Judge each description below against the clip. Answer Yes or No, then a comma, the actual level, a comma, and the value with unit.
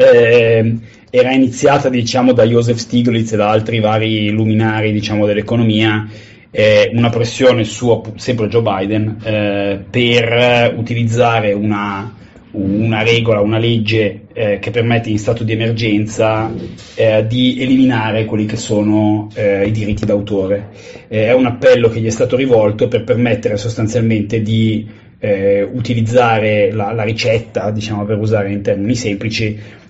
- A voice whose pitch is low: Yes, low, 110 Hz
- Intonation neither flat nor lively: No, narrow, 1.8 semitones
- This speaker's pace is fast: No, average, 140 wpm